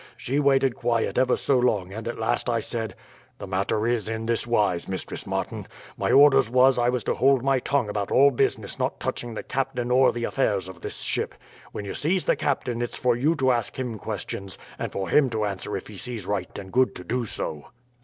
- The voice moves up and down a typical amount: Yes, average, 3.8 semitones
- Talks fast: Yes, fast, 225 wpm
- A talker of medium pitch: No, low, 120 Hz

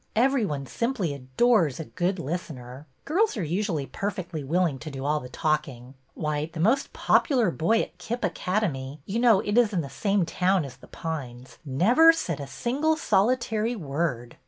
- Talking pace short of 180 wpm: No, average, 185 wpm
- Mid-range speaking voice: Yes, medium, 175 Hz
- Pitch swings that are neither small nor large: No, wide, 7.9 semitones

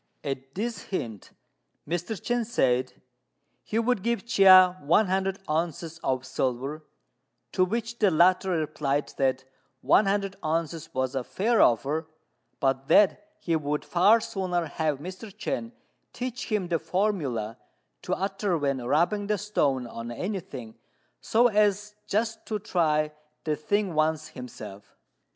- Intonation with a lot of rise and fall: Yes, wide, 6.5 semitones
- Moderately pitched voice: Yes, medium, 170 Hz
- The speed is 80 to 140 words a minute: Yes, slow, 135 wpm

